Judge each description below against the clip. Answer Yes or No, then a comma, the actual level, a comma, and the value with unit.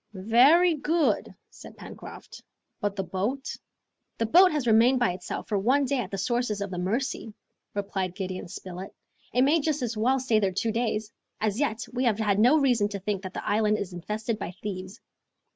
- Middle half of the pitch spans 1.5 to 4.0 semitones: No, average, 4.4 semitones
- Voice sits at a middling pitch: No, high, 220 Hz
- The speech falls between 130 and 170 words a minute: No, average, 195 wpm